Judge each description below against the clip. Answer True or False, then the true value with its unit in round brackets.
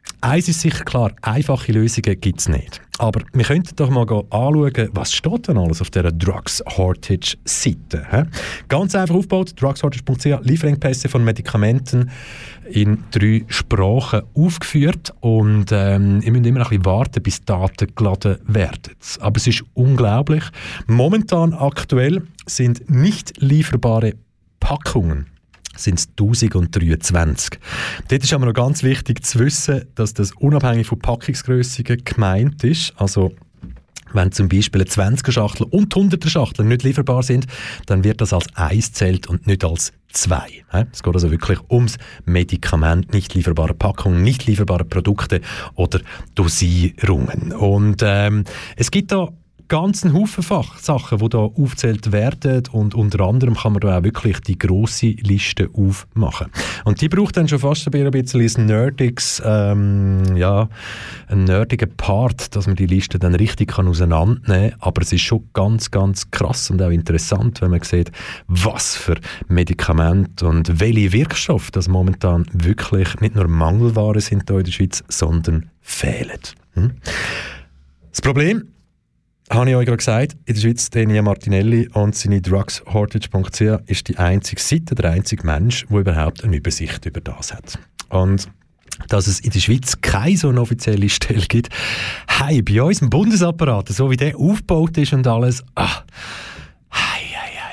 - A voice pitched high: False (110 Hz)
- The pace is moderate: True (150 wpm)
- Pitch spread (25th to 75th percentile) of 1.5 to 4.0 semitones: False (5.2 semitones)